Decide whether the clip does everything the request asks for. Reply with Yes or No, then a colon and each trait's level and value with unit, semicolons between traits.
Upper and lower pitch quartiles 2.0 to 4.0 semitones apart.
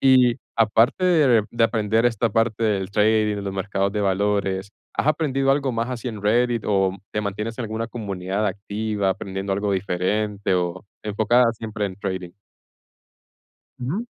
Yes: average, 2.9 semitones